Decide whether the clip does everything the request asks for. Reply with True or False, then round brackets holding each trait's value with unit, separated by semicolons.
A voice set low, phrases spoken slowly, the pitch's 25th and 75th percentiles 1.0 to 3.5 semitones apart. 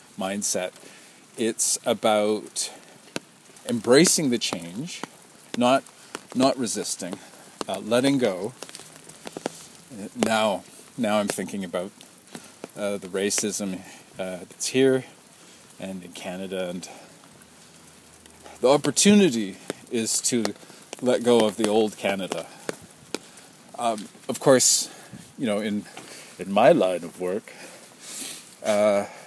True (105 Hz; 100 wpm; 2.9 semitones)